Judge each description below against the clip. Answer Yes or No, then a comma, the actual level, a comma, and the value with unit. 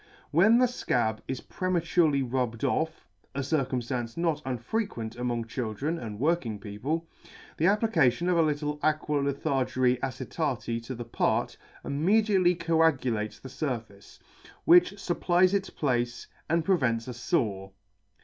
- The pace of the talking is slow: Yes, slow, 130 wpm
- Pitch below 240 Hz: Yes, medium, 140 Hz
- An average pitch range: No, wide, 5.8 semitones